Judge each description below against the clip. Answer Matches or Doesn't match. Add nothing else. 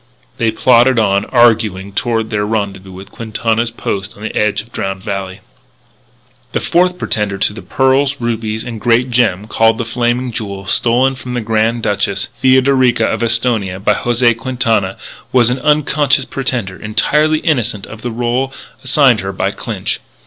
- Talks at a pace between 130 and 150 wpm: Doesn't match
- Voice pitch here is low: Matches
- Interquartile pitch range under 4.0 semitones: Matches